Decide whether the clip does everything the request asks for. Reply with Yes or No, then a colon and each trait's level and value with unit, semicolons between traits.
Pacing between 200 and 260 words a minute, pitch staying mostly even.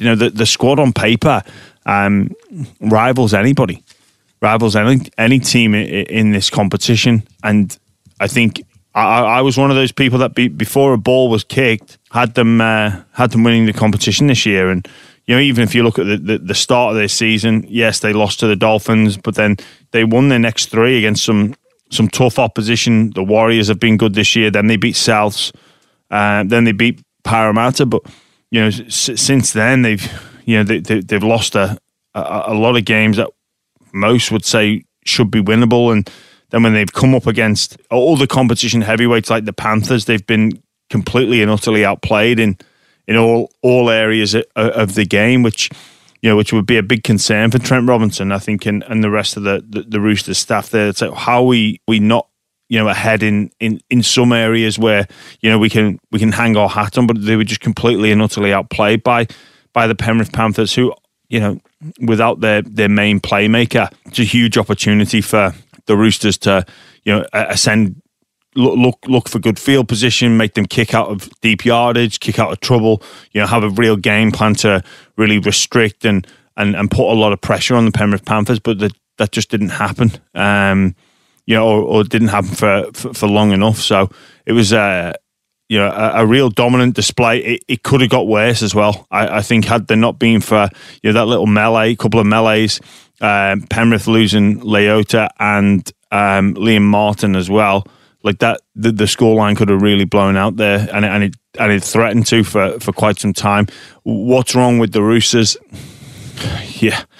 Yes: fast, 205 wpm; narrow, 2.0 semitones